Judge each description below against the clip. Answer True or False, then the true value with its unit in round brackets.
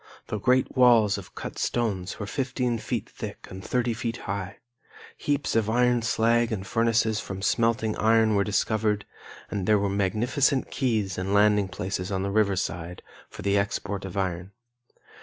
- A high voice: False (105 Hz)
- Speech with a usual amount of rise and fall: True (3.0 semitones)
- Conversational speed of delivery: True (165 wpm)